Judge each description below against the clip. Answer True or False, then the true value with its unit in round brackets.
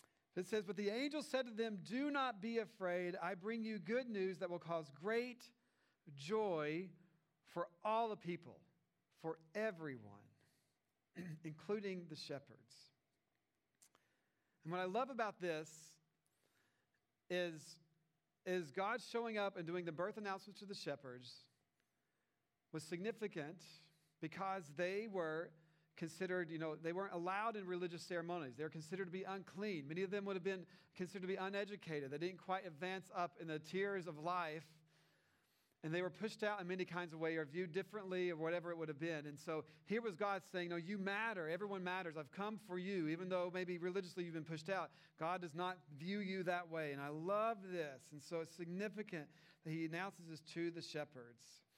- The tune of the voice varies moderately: True (3.6 semitones)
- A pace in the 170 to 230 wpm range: True (180 wpm)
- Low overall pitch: False (175 Hz)